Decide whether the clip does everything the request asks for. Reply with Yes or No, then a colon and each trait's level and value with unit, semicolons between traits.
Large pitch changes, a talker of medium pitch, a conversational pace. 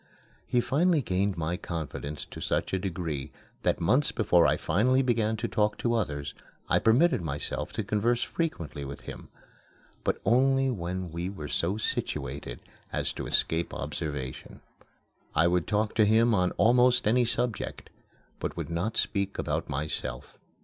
No: wide, 6.4 semitones; low, 100 Hz; average, 155 wpm